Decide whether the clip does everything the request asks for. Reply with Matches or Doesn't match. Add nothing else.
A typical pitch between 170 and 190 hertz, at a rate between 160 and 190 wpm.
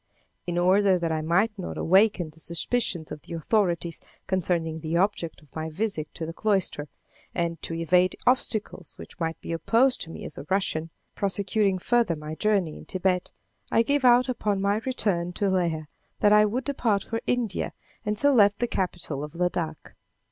Matches